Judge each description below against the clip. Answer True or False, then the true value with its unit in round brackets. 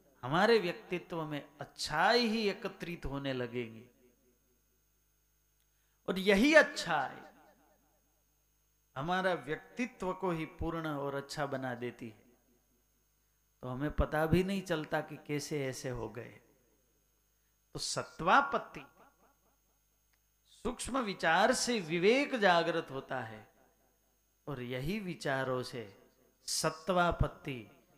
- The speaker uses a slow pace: True (100 wpm)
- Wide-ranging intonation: True (6.2 semitones)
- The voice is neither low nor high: True (150 Hz)